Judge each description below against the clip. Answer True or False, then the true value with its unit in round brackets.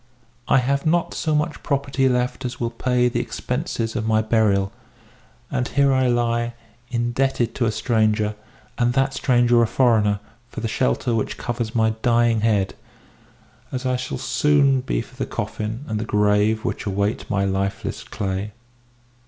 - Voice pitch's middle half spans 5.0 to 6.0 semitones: False (2.8 semitones)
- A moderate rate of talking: True (160 wpm)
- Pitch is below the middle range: True (120 Hz)